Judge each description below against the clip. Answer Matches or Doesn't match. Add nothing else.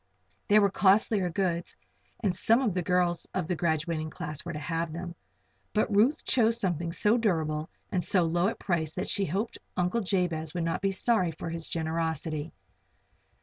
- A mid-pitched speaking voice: Matches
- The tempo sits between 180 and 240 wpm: Matches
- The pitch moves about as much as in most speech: Matches